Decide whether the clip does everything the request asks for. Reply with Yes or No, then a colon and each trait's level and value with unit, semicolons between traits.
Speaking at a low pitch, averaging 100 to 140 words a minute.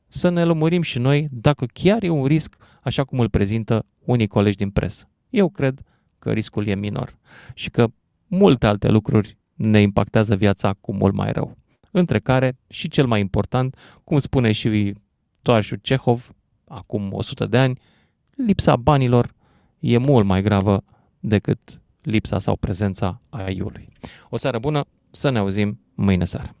No: low, 115 Hz; average, 160 wpm